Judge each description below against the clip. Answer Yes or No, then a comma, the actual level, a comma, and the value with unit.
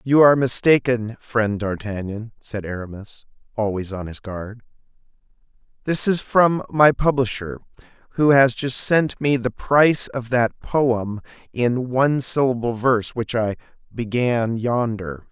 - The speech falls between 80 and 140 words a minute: Yes, slow, 135 wpm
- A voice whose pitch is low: Yes, low, 120 Hz